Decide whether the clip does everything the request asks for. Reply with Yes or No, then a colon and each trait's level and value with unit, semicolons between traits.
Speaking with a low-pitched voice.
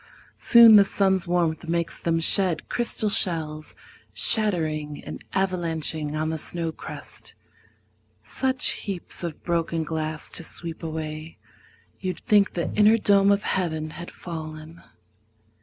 No: medium, 170 Hz